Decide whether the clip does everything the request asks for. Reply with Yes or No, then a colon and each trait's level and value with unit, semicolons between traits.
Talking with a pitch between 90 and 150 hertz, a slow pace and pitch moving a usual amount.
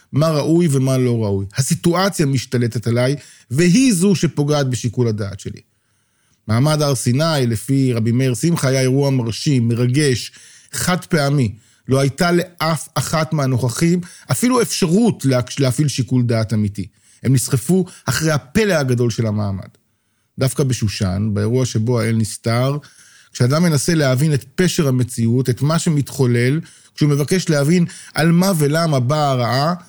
No: low, 135 Hz; average, 135 wpm; average, 4.9 semitones